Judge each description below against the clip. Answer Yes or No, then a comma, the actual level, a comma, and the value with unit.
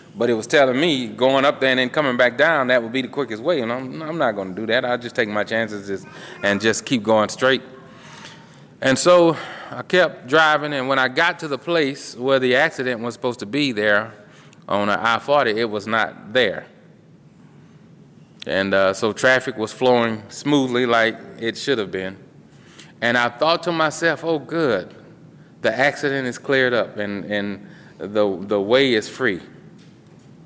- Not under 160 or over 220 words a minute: Yes, average, 190 wpm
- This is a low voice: Yes, low, 125 Hz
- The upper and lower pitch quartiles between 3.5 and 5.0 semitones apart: Yes, average, 3.9 semitones